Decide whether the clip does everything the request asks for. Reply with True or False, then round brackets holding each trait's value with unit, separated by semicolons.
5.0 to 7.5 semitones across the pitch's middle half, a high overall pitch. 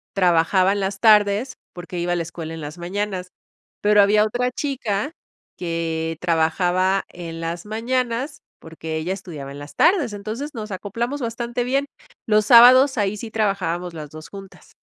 True (5.3 semitones; 195 Hz)